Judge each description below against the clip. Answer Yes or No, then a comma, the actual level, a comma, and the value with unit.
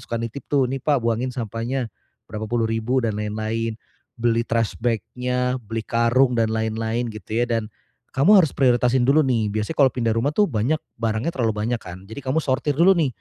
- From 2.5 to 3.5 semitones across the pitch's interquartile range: Yes, average, 2.8 semitones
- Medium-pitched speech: No, low, 120 Hz